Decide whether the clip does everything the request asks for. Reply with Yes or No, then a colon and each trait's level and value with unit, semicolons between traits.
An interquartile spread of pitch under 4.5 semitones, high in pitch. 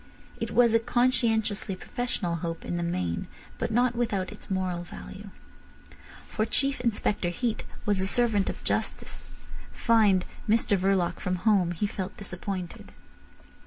Yes: average, 3.9 semitones; high, 200 Hz